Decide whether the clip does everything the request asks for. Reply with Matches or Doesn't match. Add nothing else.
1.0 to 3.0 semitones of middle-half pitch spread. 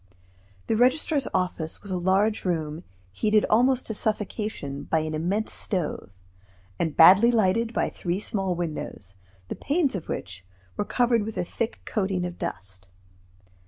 Doesn't match